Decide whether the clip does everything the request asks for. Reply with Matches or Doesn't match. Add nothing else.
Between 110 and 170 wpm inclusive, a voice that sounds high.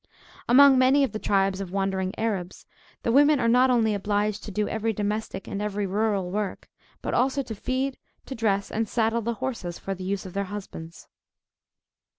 Doesn't match